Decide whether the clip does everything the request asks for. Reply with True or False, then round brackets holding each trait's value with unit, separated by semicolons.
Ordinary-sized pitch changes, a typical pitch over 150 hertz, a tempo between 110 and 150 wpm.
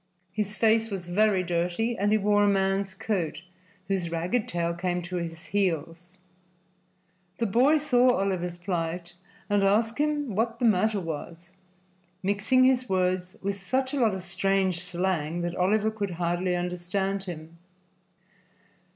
True (3.6 semitones; 190 Hz; 145 wpm)